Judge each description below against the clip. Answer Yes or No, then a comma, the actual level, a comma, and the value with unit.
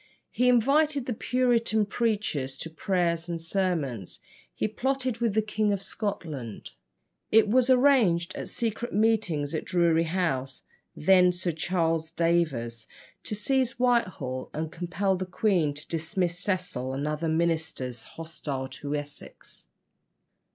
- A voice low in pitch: No, medium, 175 Hz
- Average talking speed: No, slow, 130 wpm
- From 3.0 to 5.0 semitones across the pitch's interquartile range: No, wide, 5.6 semitones